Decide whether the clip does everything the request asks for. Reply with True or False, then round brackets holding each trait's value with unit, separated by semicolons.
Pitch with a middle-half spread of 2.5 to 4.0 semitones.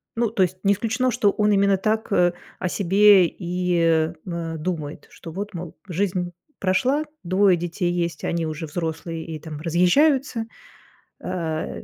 True (3.6 semitones)